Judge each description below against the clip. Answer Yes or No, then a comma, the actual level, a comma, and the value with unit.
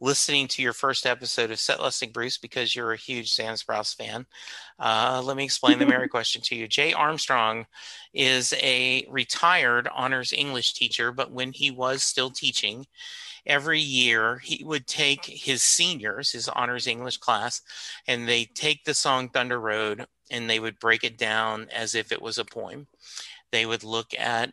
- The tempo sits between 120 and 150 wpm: No, average, 180 wpm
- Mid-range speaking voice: No, low, 125 Hz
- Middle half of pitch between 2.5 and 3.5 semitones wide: Yes, average, 3.2 semitones